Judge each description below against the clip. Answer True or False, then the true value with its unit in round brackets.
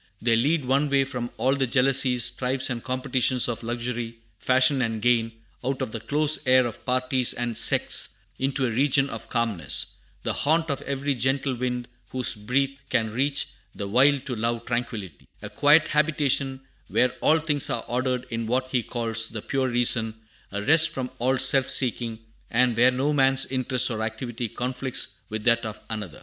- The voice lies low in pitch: True (125 Hz)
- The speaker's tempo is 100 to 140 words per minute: False (180 wpm)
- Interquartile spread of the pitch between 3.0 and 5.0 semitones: False (2.5 semitones)